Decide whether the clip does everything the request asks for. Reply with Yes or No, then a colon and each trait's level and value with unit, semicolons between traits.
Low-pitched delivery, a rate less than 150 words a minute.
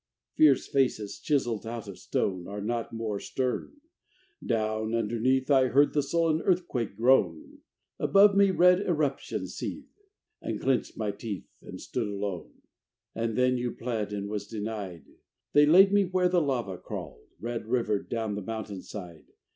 No: low, 115 Hz; average, 155 wpm